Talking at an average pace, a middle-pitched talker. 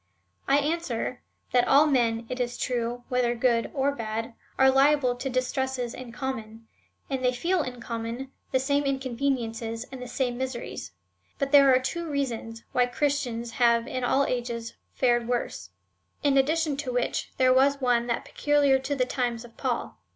No: average, 175 wpm; very high, 255 Hz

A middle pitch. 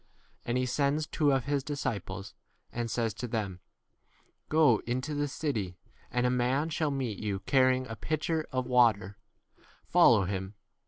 No: low, 125 Hz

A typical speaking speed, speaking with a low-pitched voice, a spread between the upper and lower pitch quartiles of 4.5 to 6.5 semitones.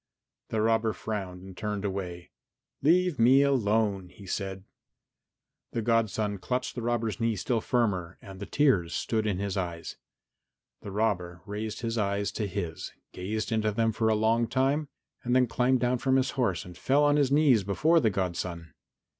No: average, 170 wpm; low, 110 Hz; average, 4.1 semitones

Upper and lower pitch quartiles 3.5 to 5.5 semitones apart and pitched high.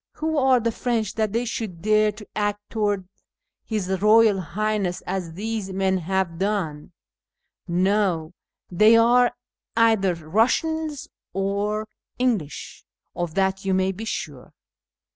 No: average, 3.1 semitones; high, 205 Hz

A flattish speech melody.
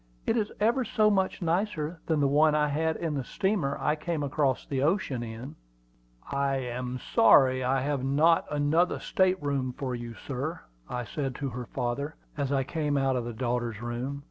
No: average, 4.0 semitones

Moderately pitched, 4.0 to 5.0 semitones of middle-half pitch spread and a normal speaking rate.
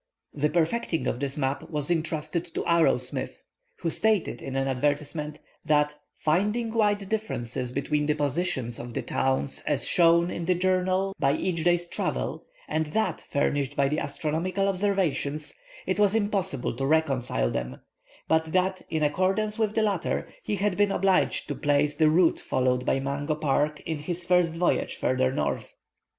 Yes: medium, 160 Hz; average, 4.5 semitones; average, 165 wpm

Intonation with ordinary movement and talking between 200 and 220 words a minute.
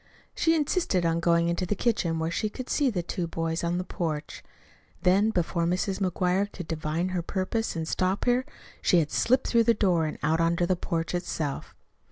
Yes: average, 3.4 semitones; fast, 205 wpm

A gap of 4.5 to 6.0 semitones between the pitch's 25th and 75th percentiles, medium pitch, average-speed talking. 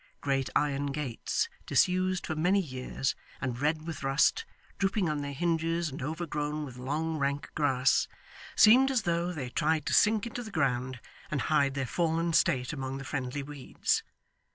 No: average, 3.8 semitones; medium, 150 Hz; average, 165 wpm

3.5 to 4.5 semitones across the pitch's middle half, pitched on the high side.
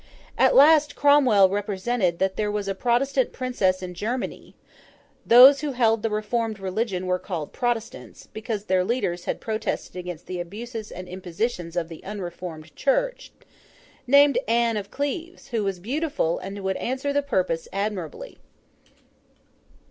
No: average, 5.1 semitones; high, 210 Hz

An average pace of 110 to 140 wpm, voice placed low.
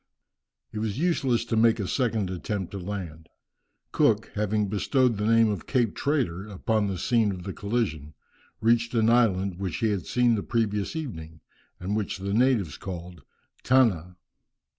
No: average, 160 wpm; low, 105 Hz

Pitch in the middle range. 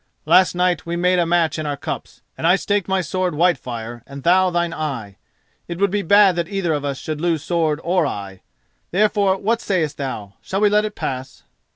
Yes: medium, 170 Hz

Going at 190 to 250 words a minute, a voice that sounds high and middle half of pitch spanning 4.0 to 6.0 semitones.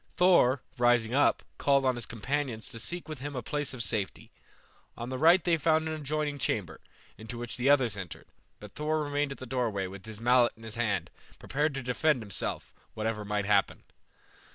No: average, 195 wpm; low, 125 Hz; average, 4.7 semitones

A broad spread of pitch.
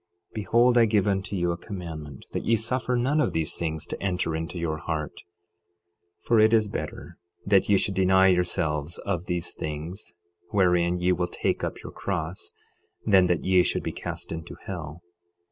No: average, 3.6 semitones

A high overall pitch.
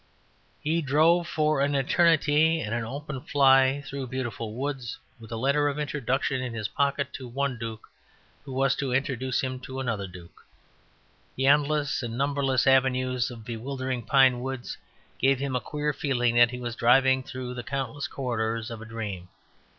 No: low, 130 Hz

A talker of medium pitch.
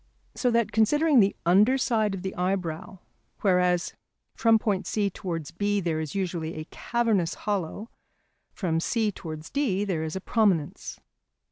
No: high, 195 Hz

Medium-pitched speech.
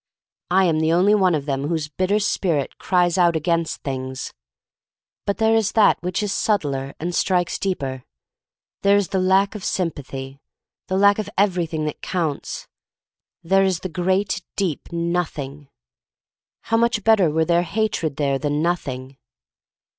Yes: medium, 175 Hz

